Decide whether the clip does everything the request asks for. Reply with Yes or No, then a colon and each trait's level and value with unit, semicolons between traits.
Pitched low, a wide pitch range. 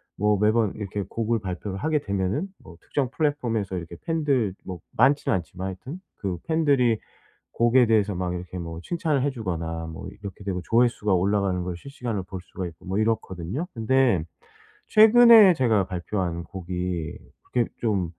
Yes: low, 105 Hz; wide, 5.8 semitones